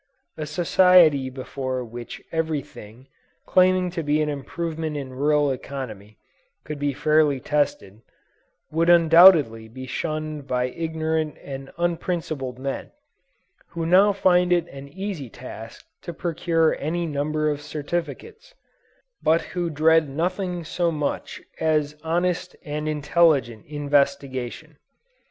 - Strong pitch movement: No, average, 3.4 semitones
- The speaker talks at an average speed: No, slow, 120 wpm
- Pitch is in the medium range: Yes, medium, 155 Hz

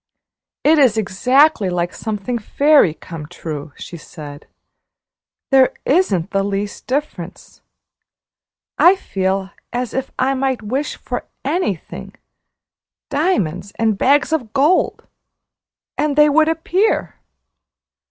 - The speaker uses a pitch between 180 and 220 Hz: No, high, 245 Hz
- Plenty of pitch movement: Yes, wide, 7.4 semitones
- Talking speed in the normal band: No, slow, 110 wpm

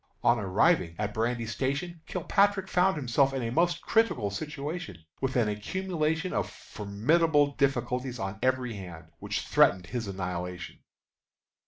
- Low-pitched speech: Yes, low, 125 Hz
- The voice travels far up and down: Yes, wide, 7.7 semitones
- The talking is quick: No, slow, 135 wpm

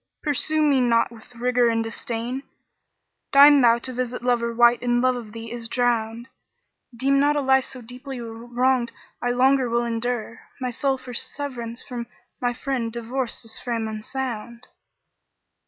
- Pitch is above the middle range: Yes, high, 245 Hz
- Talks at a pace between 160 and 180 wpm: Yes, average, 165 wpm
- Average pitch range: No, narrow, 1.9 semitones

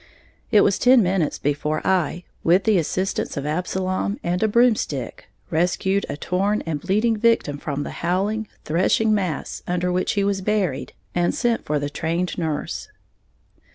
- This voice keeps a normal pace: Yes, average, 155 wpm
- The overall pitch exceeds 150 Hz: Yes, medium, 185 Hz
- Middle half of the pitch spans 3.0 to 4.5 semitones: Yes, average, 4.2 semitones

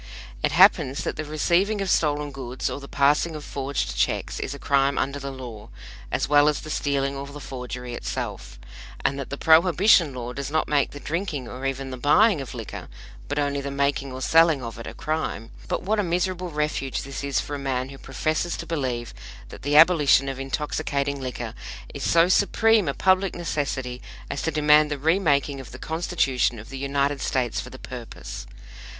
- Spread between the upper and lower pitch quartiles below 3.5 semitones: Yes, average, 2.8 semitones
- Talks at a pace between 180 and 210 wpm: Yes, average, 200 wpm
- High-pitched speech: No, medium, 140 Hz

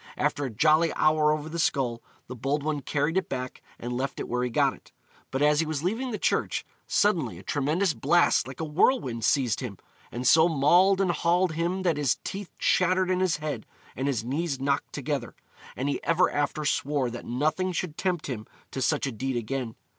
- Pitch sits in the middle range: Yes, medium, 150 Hz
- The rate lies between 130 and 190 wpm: No, fast, 205 wpm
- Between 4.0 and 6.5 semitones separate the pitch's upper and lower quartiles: Yes, average, 4.5 semitones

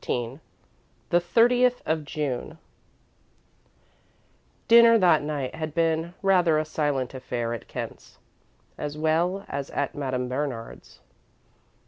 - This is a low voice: No, medium, 155 Hz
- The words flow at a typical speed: No, slow, 110 wpm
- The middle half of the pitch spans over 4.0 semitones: Yes, average, 4.4 semitones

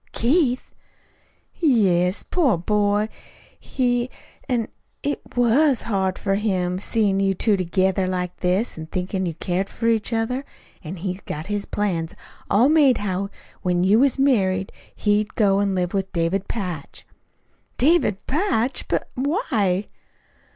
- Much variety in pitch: No, average, 4.5 semitones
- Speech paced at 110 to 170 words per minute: Yes, slow, 135 wpm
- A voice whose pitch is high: Yes, high, 205 Hz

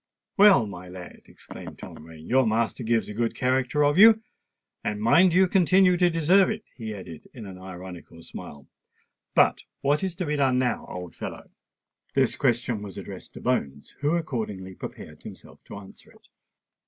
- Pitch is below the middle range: Yes, low, 120 Hz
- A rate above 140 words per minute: Yes, average, 175 wpm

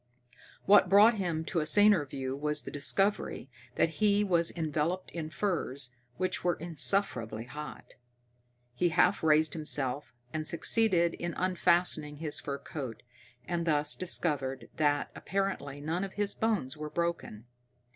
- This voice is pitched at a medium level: Yes, medium, 160 Hz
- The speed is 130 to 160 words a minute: Yes, average, 140 wpm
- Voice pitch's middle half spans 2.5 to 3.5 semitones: No, average, 4.1 semitones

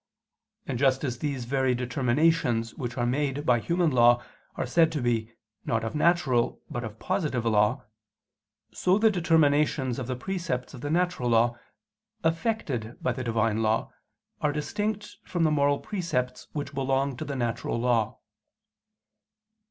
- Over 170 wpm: No, average, 150 wpm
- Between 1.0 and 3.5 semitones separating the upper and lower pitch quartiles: No, average, 4.7 semitones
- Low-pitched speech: Yes, low, 130 Hz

